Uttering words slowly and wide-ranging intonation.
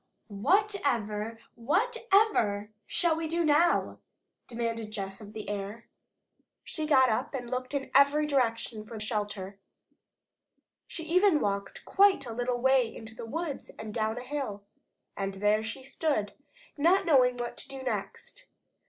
No: average, 145 wpm; wide, 5.9 semitones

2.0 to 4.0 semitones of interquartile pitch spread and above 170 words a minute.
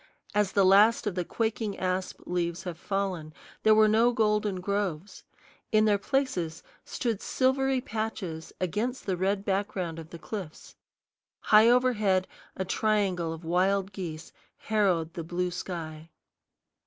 No: average, 3.6 semitones; average, 140 wpm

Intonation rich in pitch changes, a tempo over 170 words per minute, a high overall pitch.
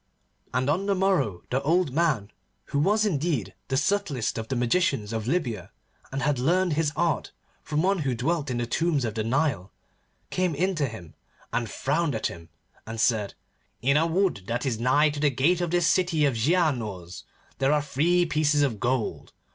No: wide, 6.2 semitones; average, 190 wpm; medium, 145 Hz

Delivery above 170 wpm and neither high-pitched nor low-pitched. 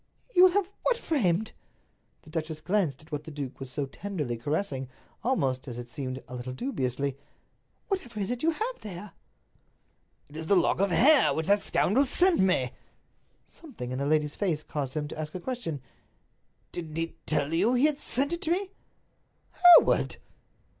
Yes: average, 180 wpm; medium, 170 Hz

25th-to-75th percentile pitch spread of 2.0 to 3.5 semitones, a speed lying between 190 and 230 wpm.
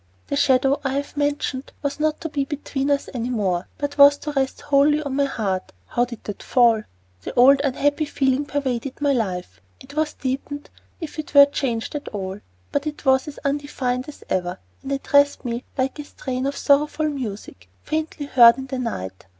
Yes: average, 2.7 semitones; average, 195 wpm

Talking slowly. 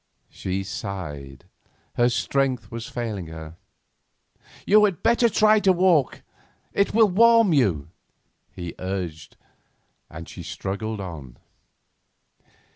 Yes: slow, 110 wpm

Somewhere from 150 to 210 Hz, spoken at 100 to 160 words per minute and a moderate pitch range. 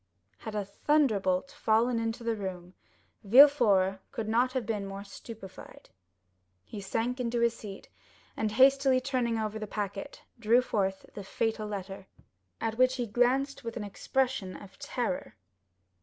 No: high, 225 Hz; average, 150 wpm; average, 3.9 semitones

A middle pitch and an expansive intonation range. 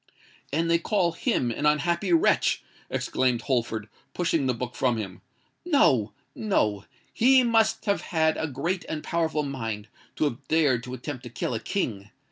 Yes: medium, 145 Hz; wide, 6.1 semitones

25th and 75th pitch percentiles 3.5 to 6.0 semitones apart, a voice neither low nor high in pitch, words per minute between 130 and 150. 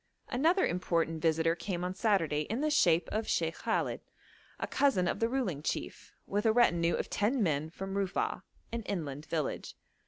No: wide, 5.4 semitones; medium, 180 Hz; average, 175 wpm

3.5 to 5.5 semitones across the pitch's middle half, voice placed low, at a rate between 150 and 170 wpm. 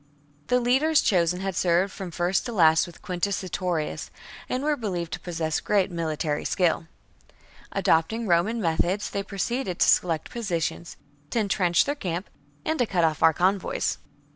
No: average, 3.8 semitones; medium, 180 Hz; average, 160 wpm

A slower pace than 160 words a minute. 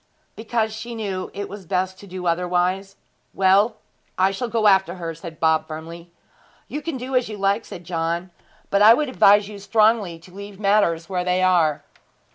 No: average, 185 wpm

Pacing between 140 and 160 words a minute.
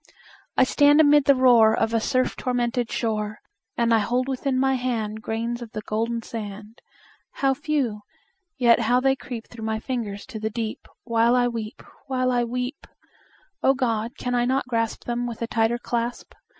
No: average, 180 wpm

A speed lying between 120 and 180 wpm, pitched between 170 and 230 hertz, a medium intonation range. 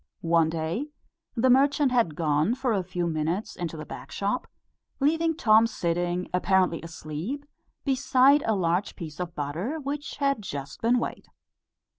No: average, 150 wpm; high, 190 Hz; wide, 7.7 semitones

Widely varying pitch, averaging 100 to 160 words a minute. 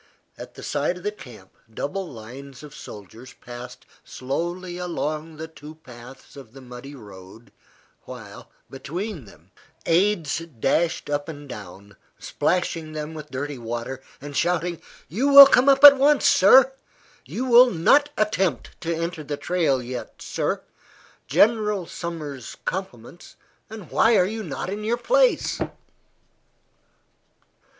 Yes: wide, 6.6 semitones; slow, 135 wpm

